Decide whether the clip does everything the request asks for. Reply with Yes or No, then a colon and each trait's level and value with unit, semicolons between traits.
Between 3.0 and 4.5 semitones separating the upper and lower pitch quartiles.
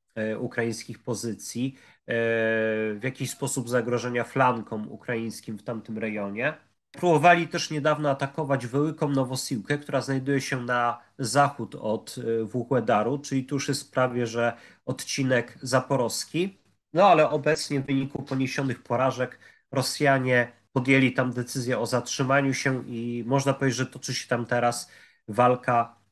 No: narrow, 2.6 semitones